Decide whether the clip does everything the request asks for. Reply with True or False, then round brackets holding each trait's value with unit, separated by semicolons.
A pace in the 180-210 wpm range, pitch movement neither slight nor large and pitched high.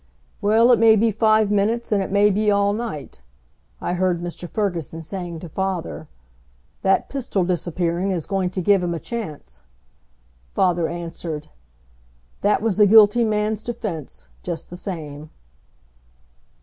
False (145 wpm; 3.7 semitones; 195 Hz)